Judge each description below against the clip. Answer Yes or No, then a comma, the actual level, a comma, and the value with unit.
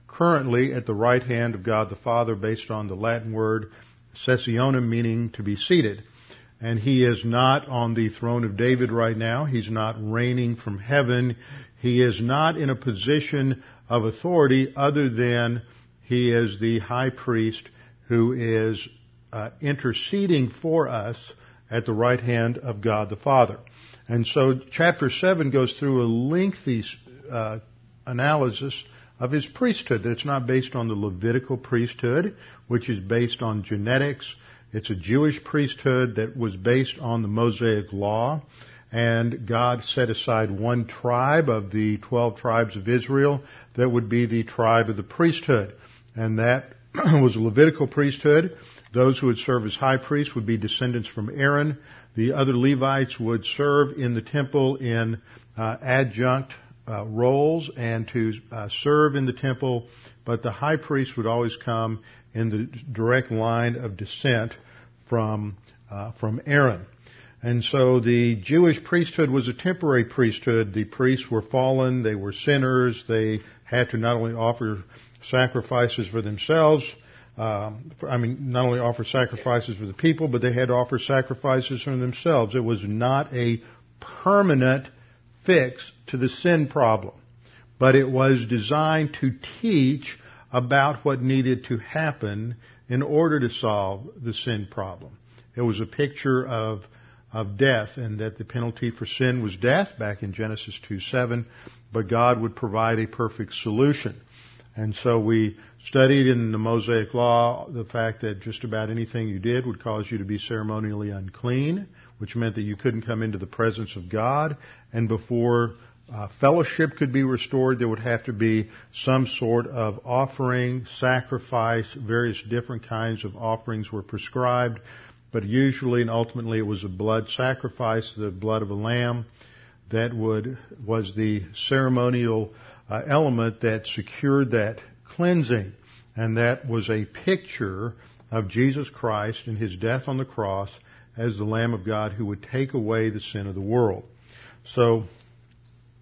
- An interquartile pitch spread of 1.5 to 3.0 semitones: Yes, narrow, 2.4 semitones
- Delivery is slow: No, average, 160 wpm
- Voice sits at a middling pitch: No, low, 120 Hz